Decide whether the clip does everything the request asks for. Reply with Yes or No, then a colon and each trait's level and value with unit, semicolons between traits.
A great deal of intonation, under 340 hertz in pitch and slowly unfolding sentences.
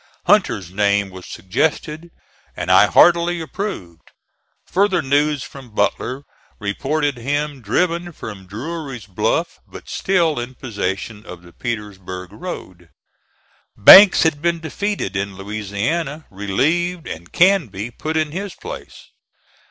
Yes: wide, 8.8 semitones; low, 135 Hz; slow, 120 wpm